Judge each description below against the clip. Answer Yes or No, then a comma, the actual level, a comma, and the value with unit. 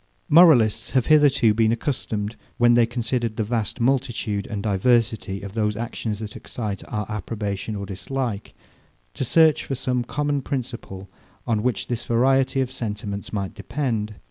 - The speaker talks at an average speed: Yes, average, 150 wpm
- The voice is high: No, low, 115 Hz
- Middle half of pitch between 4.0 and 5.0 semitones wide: No, average, 3.5 semitones